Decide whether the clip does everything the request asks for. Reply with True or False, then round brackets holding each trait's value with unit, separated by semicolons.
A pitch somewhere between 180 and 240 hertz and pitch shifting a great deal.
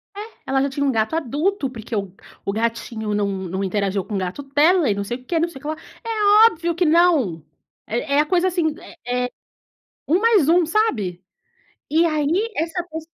False (285 Hz; 7.8 semitones)